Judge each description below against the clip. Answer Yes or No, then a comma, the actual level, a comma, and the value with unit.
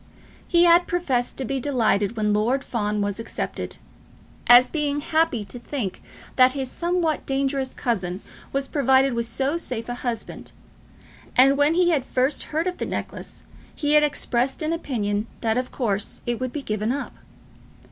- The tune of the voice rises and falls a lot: No, average, 4.2 semitones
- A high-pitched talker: Yes, very high, 260 Hz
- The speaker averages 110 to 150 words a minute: No, average, 165 wpm